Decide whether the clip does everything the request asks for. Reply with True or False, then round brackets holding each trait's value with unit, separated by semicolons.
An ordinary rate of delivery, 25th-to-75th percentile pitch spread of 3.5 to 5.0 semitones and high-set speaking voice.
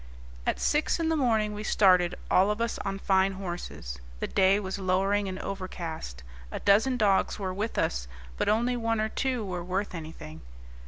False (180 wpm; 2.9 semitones; 195 Hz)